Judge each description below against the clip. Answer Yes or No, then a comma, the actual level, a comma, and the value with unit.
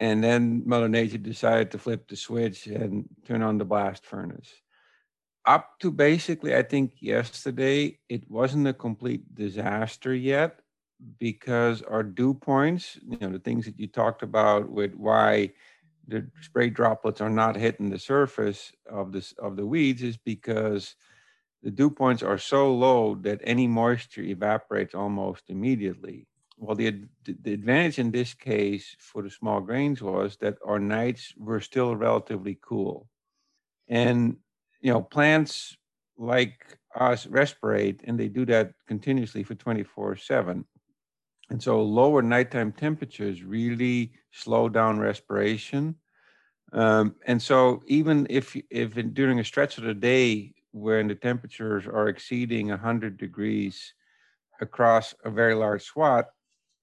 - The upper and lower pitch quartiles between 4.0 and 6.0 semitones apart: No, average, 3.2 semitones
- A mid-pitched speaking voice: No, low, 115 Hz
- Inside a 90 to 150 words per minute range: Yes, average, 145 wpm